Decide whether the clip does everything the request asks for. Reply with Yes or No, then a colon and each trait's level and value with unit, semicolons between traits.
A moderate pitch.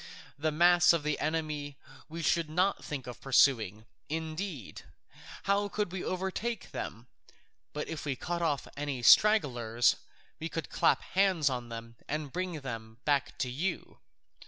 Yes: medium, 150 Hz